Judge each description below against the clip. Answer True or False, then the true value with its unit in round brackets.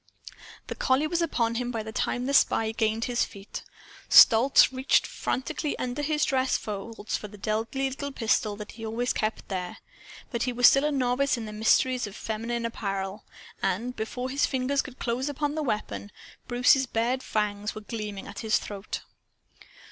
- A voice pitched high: True (235 Hz)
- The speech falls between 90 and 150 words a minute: False (180 wpm)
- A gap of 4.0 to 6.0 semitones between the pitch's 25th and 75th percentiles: False (3.4 semitones)